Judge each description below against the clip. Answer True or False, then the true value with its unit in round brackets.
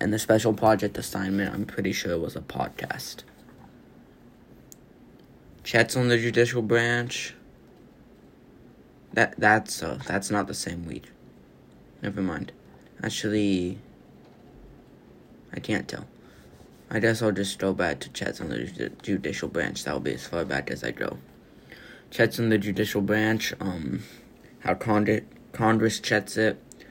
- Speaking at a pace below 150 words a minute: True (140 wpm)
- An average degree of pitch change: False (2.3 semitones)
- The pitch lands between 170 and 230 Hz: False (110 Hz)